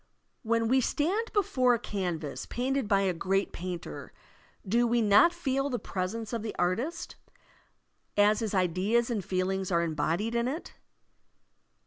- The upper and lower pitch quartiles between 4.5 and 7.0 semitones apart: Yes, average, 5.2 semitones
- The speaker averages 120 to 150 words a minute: Yes, average, 145 wpm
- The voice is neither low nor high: No, high, 220 Hz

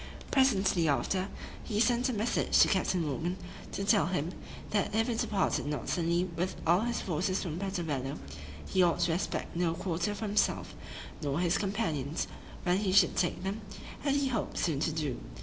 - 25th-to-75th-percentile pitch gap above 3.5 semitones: Yes, average, 4.0 semitones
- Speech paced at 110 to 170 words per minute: No, average, 185 wpm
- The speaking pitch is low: No, medium, 185 Hz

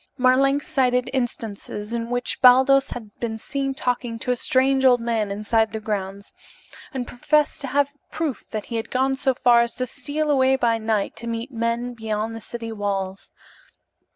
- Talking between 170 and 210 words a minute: Yes, average, 180 wpm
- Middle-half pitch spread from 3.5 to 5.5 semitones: No, average, 3.0 semitones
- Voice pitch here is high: Yes, high, 240 Hz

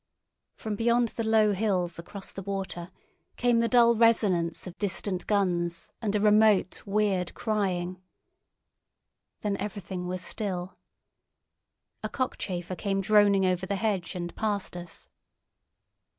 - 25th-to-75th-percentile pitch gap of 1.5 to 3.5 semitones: Yes, average, 2.9 semitones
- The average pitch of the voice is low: No, high, 195 Hz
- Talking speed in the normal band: No, slow, 125 wpm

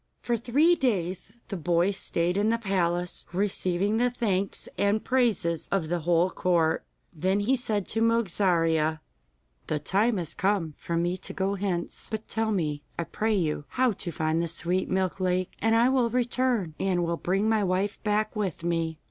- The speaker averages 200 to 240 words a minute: No, average, 180 wpm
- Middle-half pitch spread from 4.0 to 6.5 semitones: Yes, average, 4.3 semitones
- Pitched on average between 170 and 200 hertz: Yes, high, 190 Hz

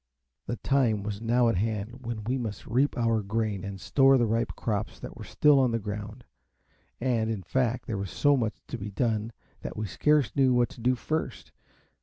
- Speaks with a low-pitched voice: Yes, low, 115 Hz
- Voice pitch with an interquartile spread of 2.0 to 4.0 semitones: Yes, average, 3.0 semitones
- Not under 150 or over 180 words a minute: No, fast, 205 wpm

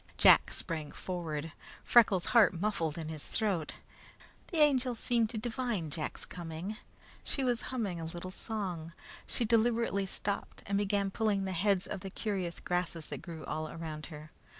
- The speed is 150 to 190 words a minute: Yes, average, 160 wpm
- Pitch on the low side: No, high, 190 Hz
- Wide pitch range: No, average, 4.9 semitones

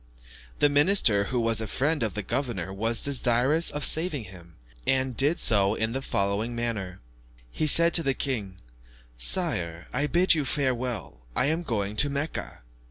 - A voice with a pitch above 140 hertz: No, low, 120 Hz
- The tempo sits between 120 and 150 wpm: No, average, 165 wpm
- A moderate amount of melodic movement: No, wide, 6.0 semitones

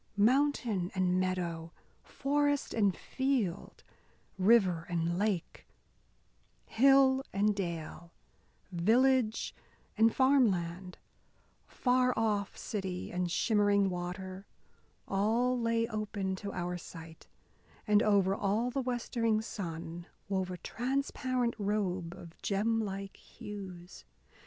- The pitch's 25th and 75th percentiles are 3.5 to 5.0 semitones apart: Yes, average, 4.4 semitones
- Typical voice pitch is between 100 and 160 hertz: No, high, 200 Hz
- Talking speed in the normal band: No, slow, 100 wpm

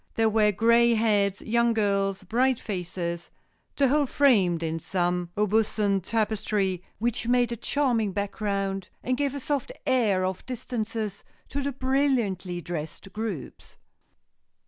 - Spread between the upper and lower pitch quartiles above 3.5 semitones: Yes, average, 3.9 semitones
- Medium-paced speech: No, slow, 125 wpm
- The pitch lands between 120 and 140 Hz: No, high, 215 Hz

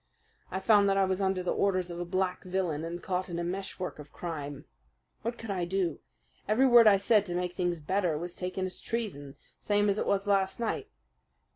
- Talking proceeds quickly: Yes, fast, 215 wpm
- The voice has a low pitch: No, medium, 185 Hz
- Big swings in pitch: No, narrow, 2.4 semitones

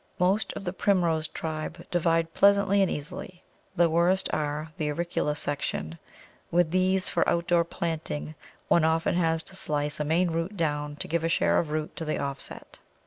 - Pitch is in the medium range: Yes, medium, 165 Hz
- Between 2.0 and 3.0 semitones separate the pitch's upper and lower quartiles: Yes, narrow, 2.5 semitones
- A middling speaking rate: Yes, average, 175 wpm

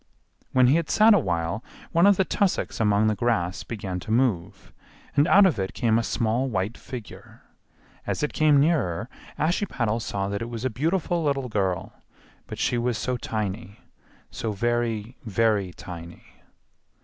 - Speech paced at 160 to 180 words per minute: Yes, average, 165 wpm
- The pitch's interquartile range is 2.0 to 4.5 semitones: No, average, 5.3 semitones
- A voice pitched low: Yes, low, 115 Hz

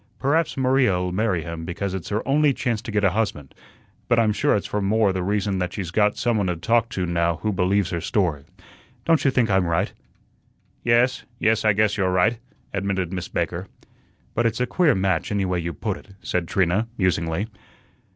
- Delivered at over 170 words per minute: Yes, average, 200 wpm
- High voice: No, low, 100 Hz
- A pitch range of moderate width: Yes, average, 3.8 semitones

